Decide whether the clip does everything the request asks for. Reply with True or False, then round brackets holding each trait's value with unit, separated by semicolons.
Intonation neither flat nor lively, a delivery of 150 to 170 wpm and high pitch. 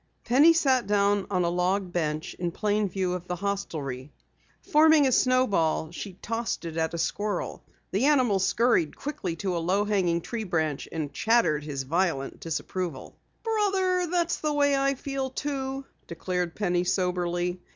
False (7.2 semitones; 160 wpm; 195 Hz)